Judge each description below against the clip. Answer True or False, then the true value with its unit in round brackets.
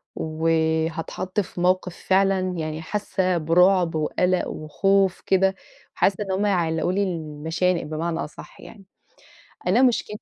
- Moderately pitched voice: True (180 Hz)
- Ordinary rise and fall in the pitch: True (3.1 semitones)